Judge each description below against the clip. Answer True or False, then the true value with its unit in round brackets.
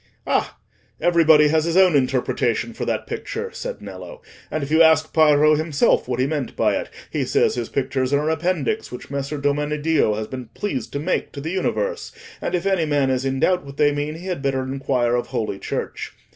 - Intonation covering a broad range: False (3.5 semitones)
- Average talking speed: False (210 wpm)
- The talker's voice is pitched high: False (150 Hz)